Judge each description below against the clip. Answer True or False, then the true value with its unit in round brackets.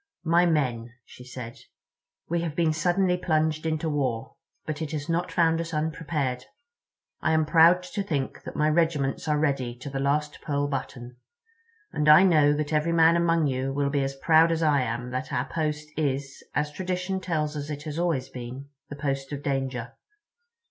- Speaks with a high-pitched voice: False (150 Hz)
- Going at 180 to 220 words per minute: True (185 wpm)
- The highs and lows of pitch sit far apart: False (3.2 semitones)